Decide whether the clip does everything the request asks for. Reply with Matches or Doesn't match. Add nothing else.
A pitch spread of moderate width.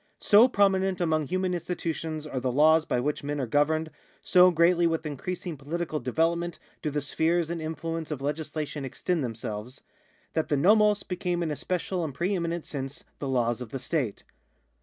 Matches